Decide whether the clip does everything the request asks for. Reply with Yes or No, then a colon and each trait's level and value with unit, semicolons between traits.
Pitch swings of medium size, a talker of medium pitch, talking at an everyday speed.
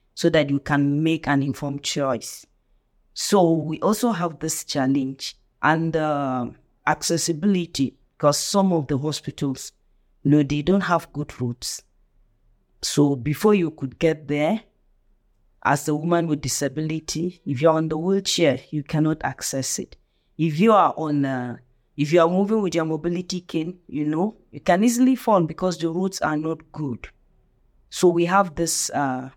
Yes: average, 3.6 semitones; medium, 155 Hz; average, 165 wpm